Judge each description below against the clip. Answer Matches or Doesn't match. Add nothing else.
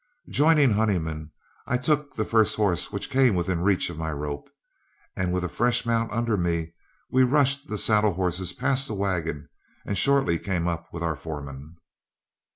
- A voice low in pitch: Matches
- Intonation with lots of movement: Matches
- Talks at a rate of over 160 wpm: Matches